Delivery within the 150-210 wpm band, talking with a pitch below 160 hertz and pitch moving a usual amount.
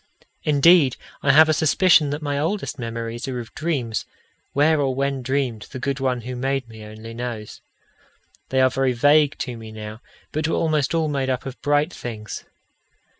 Yes: average, 180 wpm; low, 135 Hz; average, 3.8 semitones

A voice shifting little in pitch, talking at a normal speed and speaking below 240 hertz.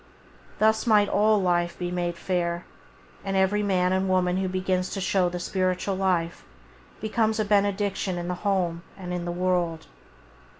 Yes: narrow, 2.0 semitones; average, 165 wpm; medium, 185 Hz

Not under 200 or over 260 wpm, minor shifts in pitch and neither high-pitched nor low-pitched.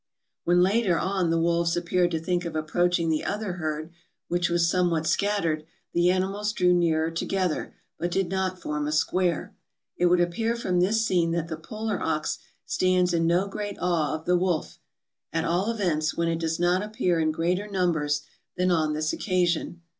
No: average, 185 wpm; narrow, 2.0 semitones; medium, 175 Hz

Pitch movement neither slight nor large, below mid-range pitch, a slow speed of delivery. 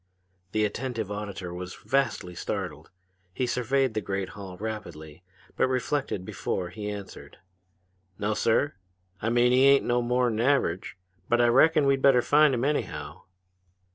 No: average, 4.7 semitones; low, 115 Hz; average, 145 wpm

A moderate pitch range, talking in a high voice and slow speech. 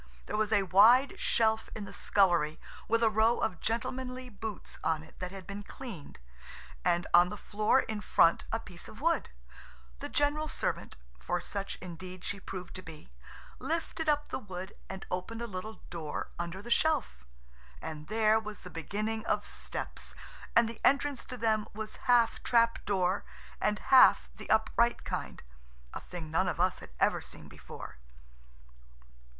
No: average, 4.6 semitones; high, 210 Hz; average, 155 wpm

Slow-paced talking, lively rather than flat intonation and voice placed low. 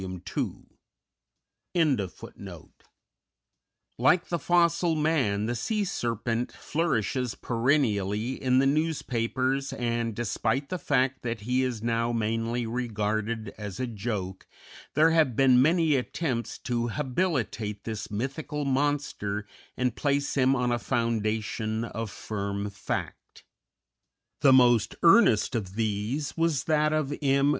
No: slow, 115 wpm; average, 4.5 semitones; low, 120 Hz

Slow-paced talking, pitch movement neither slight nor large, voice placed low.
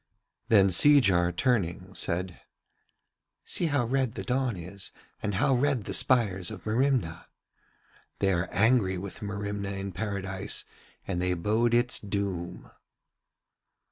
Yes: slow, 125 wpm; average, 4.5 semitones; low, 100 Hz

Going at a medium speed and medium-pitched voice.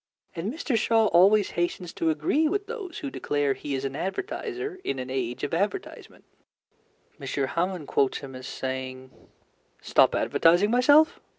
Yes: average, 155 wpm; medium, 175 Hz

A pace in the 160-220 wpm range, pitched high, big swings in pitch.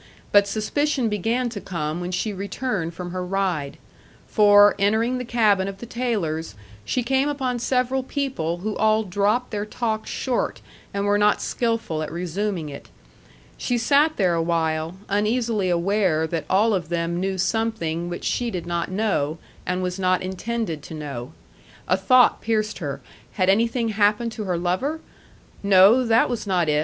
No: average, 165 wpm; high, 200 Hz; average, 4.8 semitones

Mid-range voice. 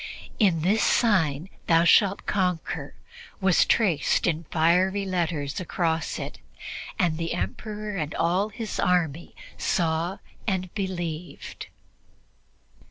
Yes: medium, 175 Hz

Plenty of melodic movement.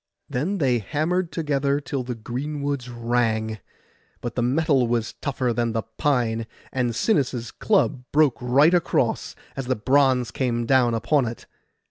No: average, 3.4 semitones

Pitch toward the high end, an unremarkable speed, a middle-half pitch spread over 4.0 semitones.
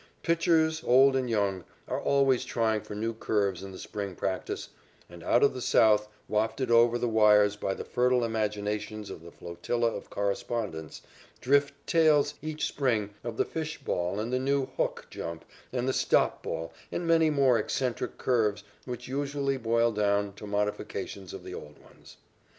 No: low, 115 Hz; average, 170 wpm; average, 4.4 semitones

